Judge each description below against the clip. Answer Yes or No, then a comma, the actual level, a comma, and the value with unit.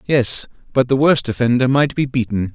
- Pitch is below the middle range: Yes, low, 125 Hz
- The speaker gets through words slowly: No, average, 190 wpm